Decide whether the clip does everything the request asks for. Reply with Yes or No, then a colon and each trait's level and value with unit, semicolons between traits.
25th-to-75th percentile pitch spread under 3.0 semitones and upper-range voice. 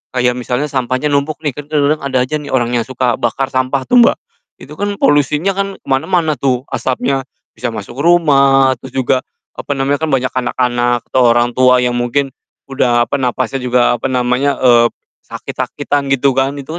No: narrow, 2.4 semitones; low, 130 Hz